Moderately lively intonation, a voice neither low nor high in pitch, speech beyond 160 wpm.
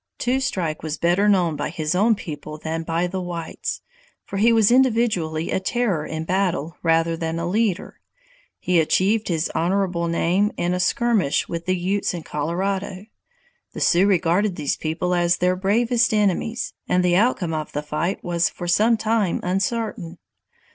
Yes: average, 3.6 semitones; medium, 180 Hz; average, 170 wpm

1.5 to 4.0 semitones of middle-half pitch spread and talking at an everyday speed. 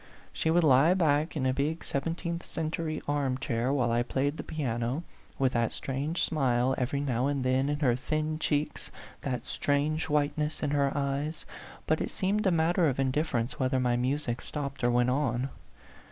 Yes: average, 3.2 semitones; average, 180 wpm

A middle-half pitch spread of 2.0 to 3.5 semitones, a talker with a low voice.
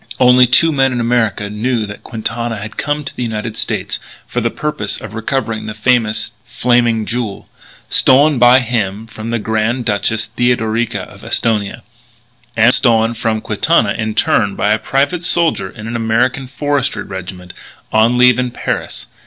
Yes: narrow, 2.4 semitones; low, 115 Hz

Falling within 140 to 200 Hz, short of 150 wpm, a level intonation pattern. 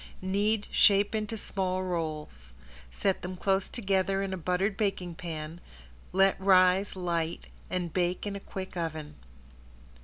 Yes: medium, 185 Hz; average, 140 wpm; narrow, 2.3 semitones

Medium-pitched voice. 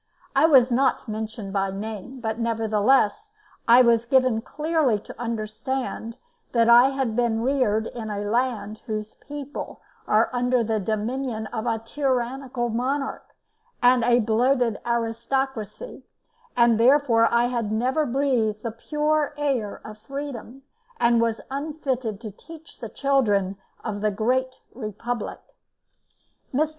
No: high, 235 Hz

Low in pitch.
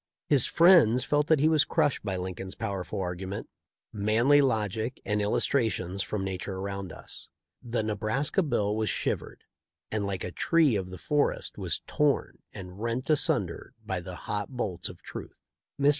Yes: low, 110 Hz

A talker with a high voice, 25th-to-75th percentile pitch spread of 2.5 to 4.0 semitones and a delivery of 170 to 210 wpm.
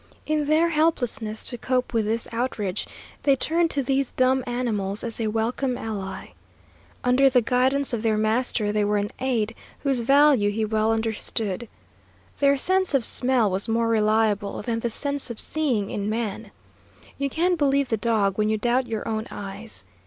Yes: high, 230 Hz; average, 3.7 semitones; average, 175 wpm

